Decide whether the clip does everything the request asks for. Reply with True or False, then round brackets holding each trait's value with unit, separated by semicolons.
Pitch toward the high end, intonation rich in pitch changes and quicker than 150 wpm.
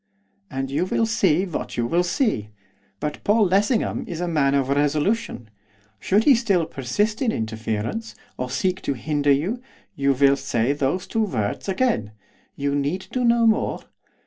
False (155 Hz; 7.4 semitones; 165 wpm)